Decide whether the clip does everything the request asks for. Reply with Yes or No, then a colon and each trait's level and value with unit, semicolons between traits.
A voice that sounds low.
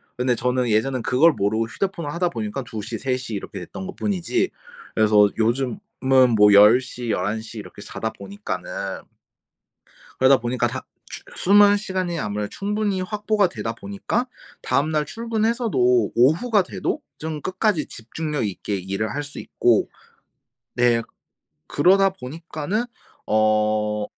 Yes: low, 130 Hz